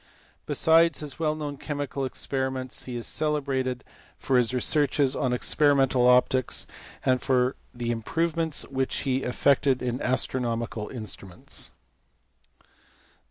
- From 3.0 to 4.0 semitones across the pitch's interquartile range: No, narrow, 2.4 semitones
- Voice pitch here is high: No, low, 130 Hz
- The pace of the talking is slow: Yes, slow, 115 wpm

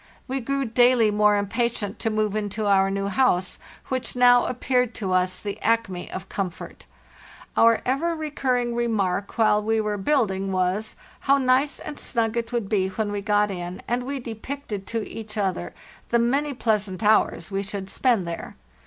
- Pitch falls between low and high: No, high, 220 Hz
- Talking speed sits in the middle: Yes, average, 170 wpm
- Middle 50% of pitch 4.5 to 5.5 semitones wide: No, average, 3.8 semitones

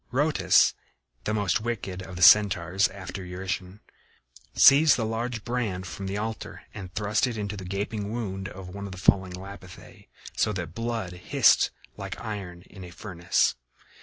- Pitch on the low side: Yes, low, 100 Hz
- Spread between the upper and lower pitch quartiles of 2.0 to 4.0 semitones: Yes, average, 3.0 semitones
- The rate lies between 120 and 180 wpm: Yes, average, 165 wpm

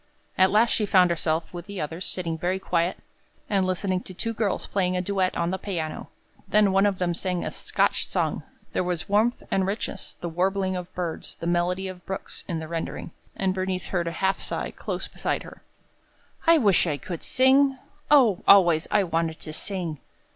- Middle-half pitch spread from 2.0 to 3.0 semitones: Yes, narrow, 2.4 semitones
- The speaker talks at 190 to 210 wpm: Yes, average, 195 wpm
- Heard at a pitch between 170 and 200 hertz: Yes, medium, 185 Hz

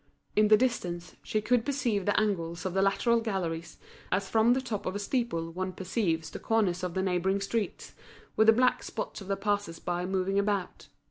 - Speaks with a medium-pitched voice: No, high, 195 Hz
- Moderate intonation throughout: Yes, average, 3.6 semitones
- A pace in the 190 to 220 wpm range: Yes, average, 200 wpm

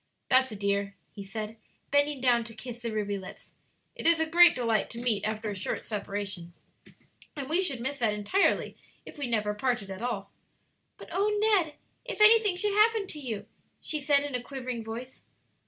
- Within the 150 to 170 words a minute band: No, average, 190 wpm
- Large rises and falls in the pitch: Yes, wide, 6.3 semitones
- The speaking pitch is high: Yes, high, 245 Hz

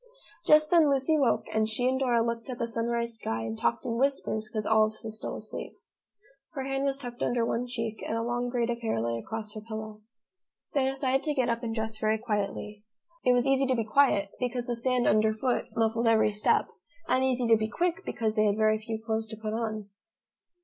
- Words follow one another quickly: Yes, fast, 220 wpm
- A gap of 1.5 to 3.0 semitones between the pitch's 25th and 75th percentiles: Yes, average, 2.7 semitones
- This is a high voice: Yes, high, 230 Hz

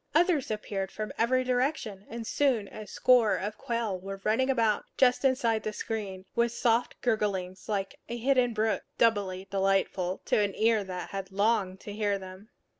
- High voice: Yes, high, 215 Hz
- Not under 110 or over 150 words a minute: No, average, 170 wpm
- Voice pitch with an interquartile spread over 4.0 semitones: No, average, 3.4 semitones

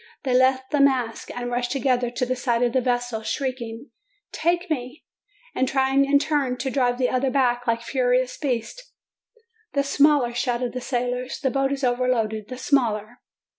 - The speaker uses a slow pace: No, average, 175 wpm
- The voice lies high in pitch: Yes, very high, 255 Hz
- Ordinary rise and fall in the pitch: No, narrow, 1.9 semitones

